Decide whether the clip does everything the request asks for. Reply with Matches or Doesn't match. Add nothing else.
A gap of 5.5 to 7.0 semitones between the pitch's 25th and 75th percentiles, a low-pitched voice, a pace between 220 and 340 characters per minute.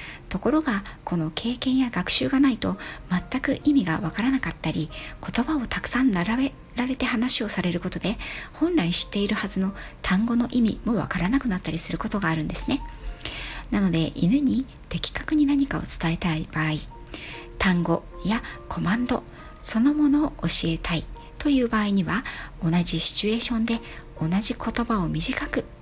Doesn't match